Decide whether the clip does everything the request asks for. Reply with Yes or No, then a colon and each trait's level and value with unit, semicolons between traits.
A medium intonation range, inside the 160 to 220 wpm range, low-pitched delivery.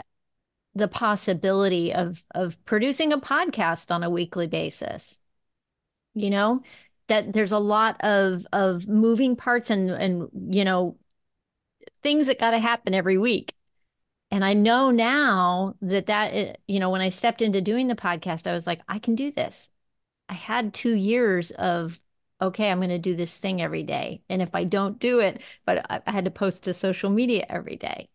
No: average, 3.8 semitones; average, 180 wpm; high, 200 Hz